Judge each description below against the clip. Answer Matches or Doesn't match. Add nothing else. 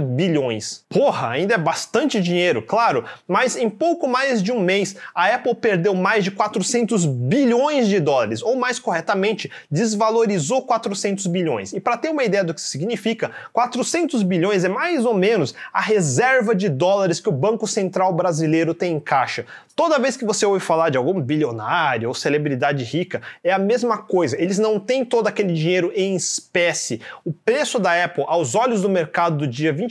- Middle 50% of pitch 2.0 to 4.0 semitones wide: Doesn't match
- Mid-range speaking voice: Doesn't match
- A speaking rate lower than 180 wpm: Doesn't match